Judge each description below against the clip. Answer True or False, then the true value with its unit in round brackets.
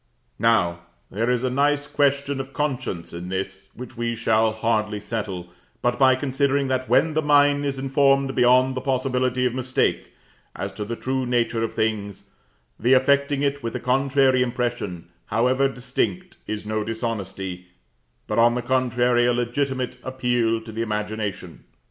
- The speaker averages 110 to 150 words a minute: False (160 wpm)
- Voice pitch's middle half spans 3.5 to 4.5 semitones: False (3.1 semitones)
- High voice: False (125 Hz)